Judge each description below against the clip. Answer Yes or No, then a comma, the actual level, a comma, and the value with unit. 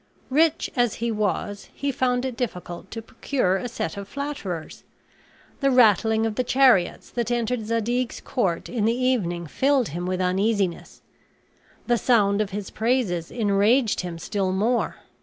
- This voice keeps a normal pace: Yes, average, 155 wpm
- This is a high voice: Yes, high, 225 Hz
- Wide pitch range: No, average, 4.4 semitones